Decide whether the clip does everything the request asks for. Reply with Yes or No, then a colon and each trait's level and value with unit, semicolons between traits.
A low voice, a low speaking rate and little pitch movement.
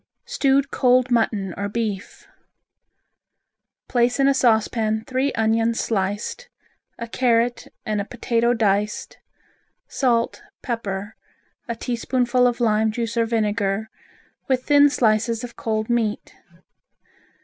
No: high, 230 Hz; slow, 115 wpm; narrow, 2.3 semitones